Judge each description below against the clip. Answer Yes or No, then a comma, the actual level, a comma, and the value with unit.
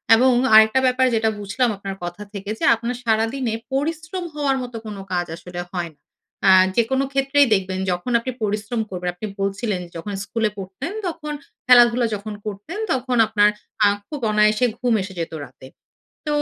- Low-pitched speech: No, high, 220 Hz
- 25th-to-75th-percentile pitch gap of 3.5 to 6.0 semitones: Yes, average, 4.6 semitones